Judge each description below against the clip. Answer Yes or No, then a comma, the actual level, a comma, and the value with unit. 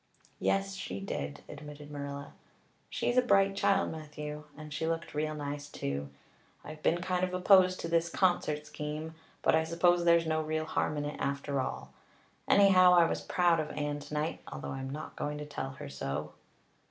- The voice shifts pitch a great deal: No, average, 3.1 semitones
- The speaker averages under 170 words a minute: No, average, 180 wpm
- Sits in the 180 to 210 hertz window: No, medium, 155 Hz